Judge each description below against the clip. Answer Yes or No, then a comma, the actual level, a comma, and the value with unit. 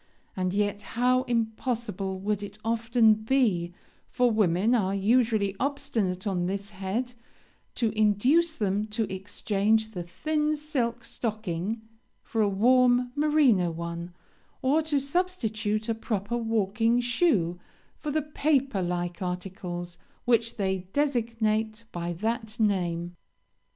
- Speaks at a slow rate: Yes, slow, 120 wpm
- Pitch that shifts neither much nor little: Yes, average, 4.3 semitones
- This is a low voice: No, high, 220 Hz